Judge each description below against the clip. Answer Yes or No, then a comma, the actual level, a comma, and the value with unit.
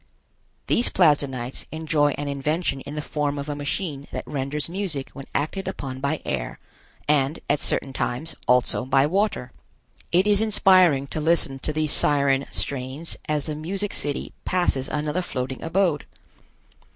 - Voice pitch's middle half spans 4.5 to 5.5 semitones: No, average, 3.3 semitones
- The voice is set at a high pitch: No, medium, 150 Hz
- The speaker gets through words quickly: No, average, 150 wpm